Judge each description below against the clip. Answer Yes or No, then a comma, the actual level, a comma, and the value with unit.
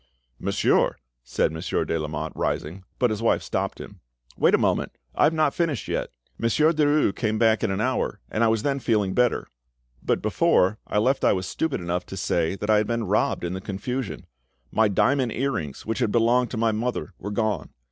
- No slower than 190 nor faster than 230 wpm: Yes, fast, 205 wpm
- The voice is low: Yes, low, 110 Hz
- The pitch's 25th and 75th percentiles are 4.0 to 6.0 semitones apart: Yes, average, 4.6 semitones